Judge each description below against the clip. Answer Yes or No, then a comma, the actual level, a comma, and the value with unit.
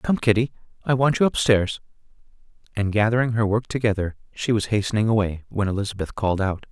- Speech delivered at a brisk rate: No, average, 180 wpm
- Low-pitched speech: Yes, low, 110 Hz